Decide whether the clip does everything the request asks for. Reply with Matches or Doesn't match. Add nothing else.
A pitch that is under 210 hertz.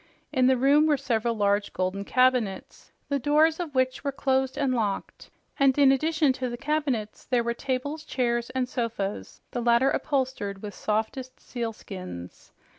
Doesn't match